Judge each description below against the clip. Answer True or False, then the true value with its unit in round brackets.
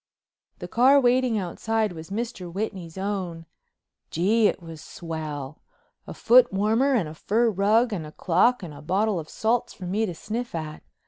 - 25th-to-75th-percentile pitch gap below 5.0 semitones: False (5.5 semitones)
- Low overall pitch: False (200 Hz)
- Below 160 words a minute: False (170 wpm)